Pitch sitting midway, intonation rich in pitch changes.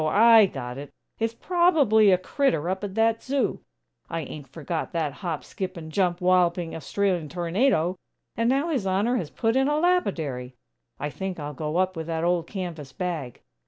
Yes: medium, 180 Hz; wide, 5.7 semitones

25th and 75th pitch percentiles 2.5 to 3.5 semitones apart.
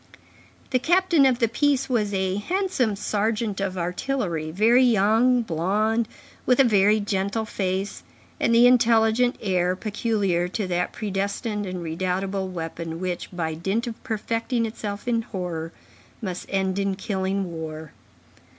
No: average, 3.9 semitones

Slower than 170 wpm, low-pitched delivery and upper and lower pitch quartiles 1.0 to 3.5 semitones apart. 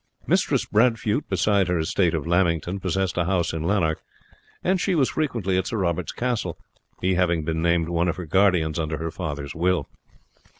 No: average, 180 wpm; very low, 90 Hz; average, 3.1 semitones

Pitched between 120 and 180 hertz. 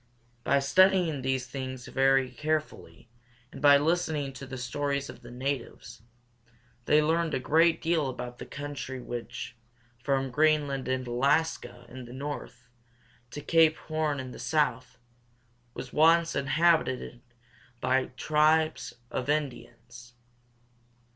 Yes: medium, 140 Hz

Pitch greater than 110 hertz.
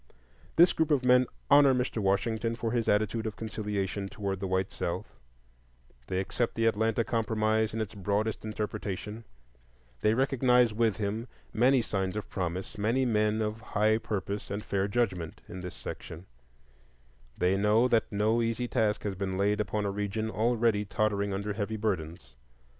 No: low, 105 Hz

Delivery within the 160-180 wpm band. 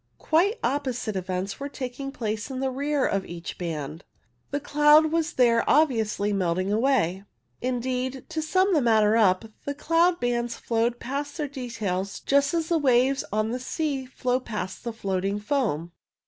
Yes: average, 165 wpm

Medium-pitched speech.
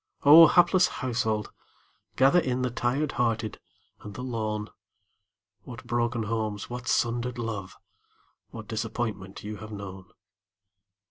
No: low, 115 Hz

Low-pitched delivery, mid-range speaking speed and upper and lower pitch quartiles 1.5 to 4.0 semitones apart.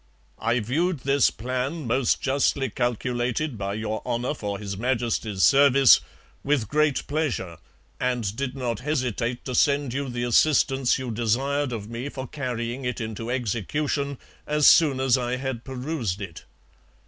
Yes: low, 125 Hz; average, 150 wpm; average, 3.1 semitones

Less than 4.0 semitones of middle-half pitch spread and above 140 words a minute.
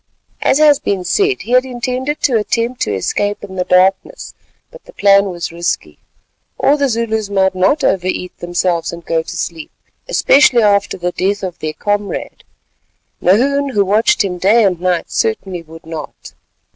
No: average, 5.2 semitones; average, 170 wpm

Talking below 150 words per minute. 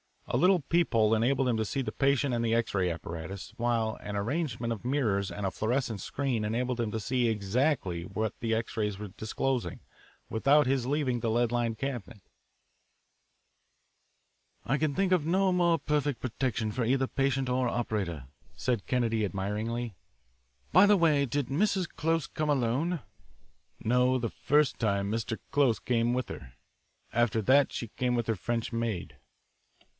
No: average, 165 wpm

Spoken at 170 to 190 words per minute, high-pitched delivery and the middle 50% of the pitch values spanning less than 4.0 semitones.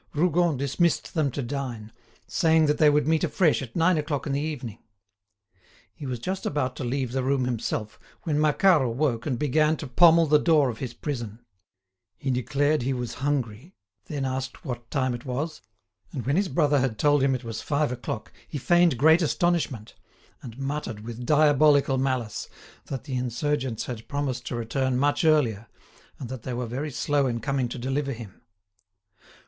No: average, 180 wpm; low, 135 Hz; average, 3.5 semitones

